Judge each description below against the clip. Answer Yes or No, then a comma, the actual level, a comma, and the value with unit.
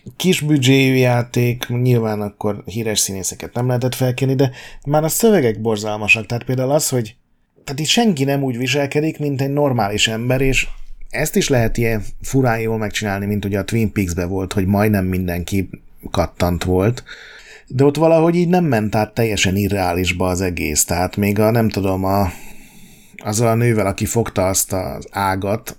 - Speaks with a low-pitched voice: Yes, low, 110 Hz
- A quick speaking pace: Yes, fast, 170 wpm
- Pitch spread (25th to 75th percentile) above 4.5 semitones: Yes, average, 5.0 semitones